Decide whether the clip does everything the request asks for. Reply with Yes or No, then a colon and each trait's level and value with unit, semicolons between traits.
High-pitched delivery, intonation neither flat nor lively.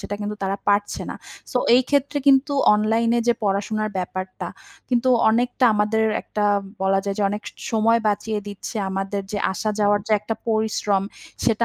No: high, 215 Hz; narrow, 2.1 semitones